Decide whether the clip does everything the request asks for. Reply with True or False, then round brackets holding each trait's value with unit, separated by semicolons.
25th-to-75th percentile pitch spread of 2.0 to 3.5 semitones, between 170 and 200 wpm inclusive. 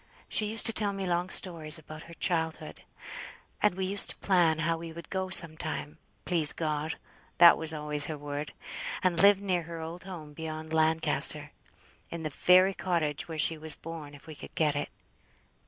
True (2.6 semitones; 185 wpm)